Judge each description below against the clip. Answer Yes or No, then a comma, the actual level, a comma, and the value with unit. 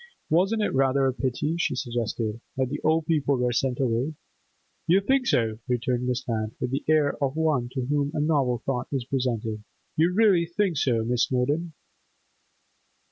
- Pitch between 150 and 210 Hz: No, low, 135 Hz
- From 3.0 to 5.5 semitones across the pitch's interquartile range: Yes, average, 4.3 semitones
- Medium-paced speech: Yes, average, 175 wpm